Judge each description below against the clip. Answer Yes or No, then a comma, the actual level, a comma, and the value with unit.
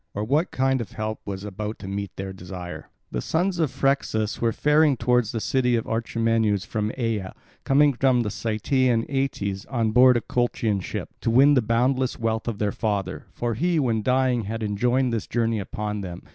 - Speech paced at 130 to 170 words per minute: No, average, 185 wpm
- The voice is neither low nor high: No, low, 115 Hz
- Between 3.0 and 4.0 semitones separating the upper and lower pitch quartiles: Yes, average, 3.7 semitones